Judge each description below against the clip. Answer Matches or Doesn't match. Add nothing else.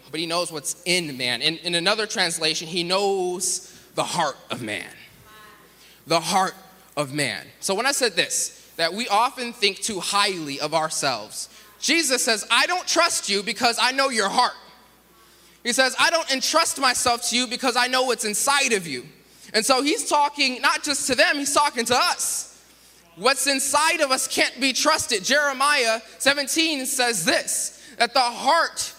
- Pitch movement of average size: Doesn't match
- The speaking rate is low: Doesn't match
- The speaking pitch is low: Doesn't match